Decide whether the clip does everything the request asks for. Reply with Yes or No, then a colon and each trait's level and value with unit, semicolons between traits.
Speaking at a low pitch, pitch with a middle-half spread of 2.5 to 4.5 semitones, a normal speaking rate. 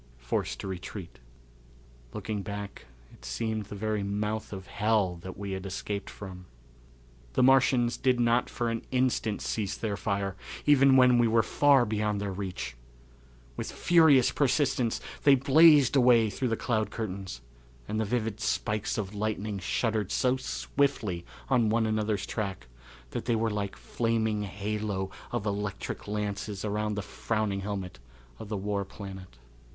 Yes: low, 105 Hz; average, 2.9 semitones; average, 155 wpm